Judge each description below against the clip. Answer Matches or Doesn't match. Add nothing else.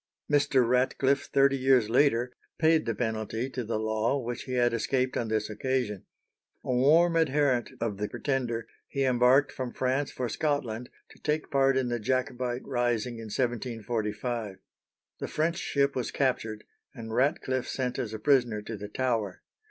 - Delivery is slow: Doesn't match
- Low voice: Matches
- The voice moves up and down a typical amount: Matches